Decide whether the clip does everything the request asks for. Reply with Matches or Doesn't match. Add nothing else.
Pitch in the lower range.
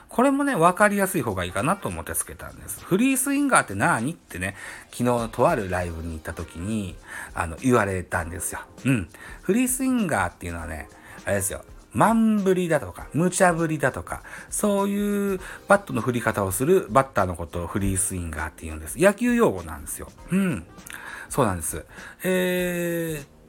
Matches